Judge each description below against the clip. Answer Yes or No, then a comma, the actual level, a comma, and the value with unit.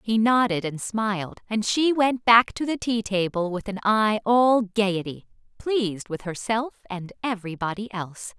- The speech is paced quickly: No, average, 165 wpm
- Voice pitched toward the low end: No, high, 210 Hz